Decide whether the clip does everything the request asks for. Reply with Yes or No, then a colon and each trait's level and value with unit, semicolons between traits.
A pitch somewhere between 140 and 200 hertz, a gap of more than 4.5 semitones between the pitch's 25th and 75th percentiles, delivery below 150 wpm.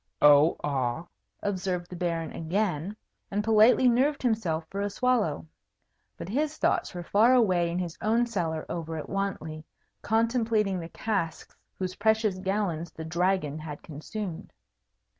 Yes: medium, 185 Hz; average, 4.9 semitones; average, 140 wpm